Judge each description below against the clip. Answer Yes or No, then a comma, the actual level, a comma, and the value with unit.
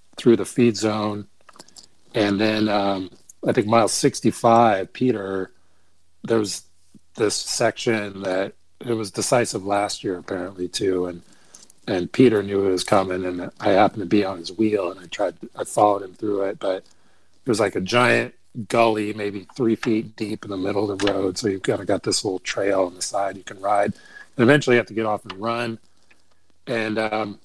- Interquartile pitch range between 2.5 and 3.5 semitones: Yes, average, 2.9 semitones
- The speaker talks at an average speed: Yes, average, 195 wpm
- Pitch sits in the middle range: No, low, 100 Hz